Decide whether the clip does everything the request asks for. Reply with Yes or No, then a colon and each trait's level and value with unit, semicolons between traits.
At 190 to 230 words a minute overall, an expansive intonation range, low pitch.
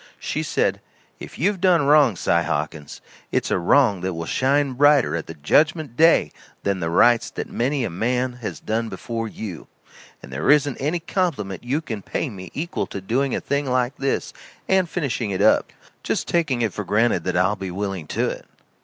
Yes: average, 195 wpm; wide, 7.3 semitones; low, 120 Hz